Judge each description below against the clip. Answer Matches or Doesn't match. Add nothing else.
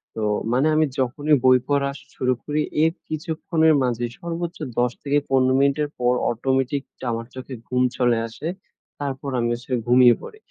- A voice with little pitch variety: Doesn't match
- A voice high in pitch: Doesn't match